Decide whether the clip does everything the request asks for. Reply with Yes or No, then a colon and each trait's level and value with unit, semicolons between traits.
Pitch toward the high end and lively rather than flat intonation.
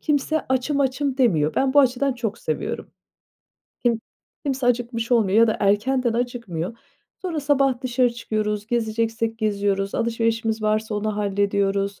No: high, 230 Hz; average, 3.5 semitones